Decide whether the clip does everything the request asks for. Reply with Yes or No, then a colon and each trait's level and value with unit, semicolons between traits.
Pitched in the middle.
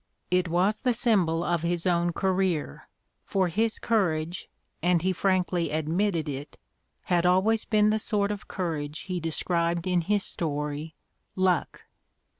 Yes: medium, 180 Hz